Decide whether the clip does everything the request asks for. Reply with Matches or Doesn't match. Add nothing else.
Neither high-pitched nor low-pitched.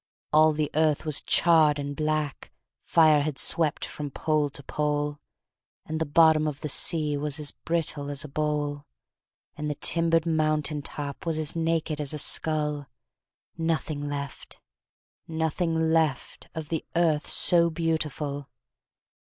Matches